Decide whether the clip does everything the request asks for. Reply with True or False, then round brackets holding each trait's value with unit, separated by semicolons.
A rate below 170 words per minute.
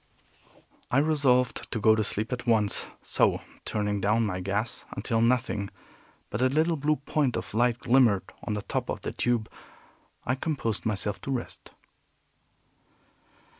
True (150 wpm)